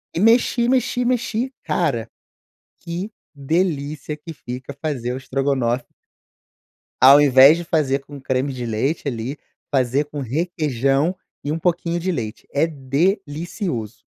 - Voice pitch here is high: No, medium, 145 Hz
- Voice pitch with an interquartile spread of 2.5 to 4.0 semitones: No, average, 4.6 semitones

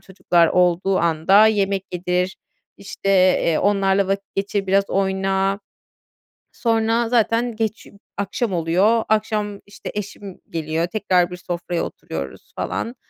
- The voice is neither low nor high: No, high, 195 Hz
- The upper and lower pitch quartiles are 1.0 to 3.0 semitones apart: Yes, average, 2.7 semitones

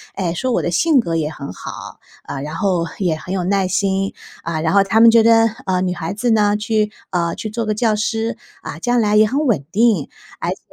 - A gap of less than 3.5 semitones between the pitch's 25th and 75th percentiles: No, average, 4.3 semitones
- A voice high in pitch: Yes, high, 200 Hz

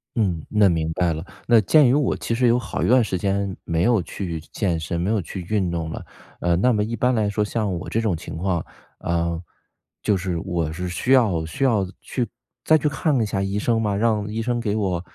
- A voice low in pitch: Yes, low, 100 Hz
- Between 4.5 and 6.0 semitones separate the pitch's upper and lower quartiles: Yes, average, 4.9 semitones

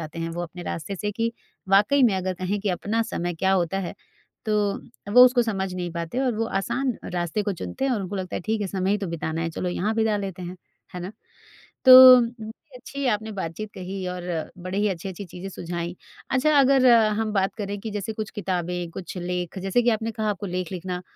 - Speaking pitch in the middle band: No, high, 195 Hz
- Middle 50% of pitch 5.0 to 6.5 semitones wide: No, average, 3.6 semitones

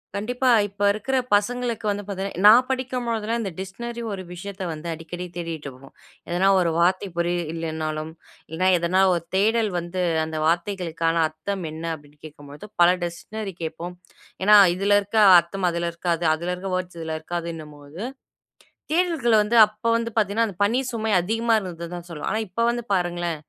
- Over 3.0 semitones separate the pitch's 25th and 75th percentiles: Yes, average, 4.2 semitones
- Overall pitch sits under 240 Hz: Yes, medium, 185 Hz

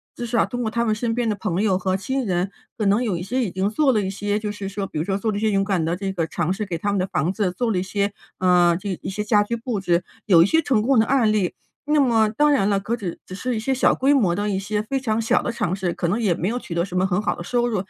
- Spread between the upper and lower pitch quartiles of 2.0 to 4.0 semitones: Yes, average, 3.6 semitones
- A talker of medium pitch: No, high, 205 Hz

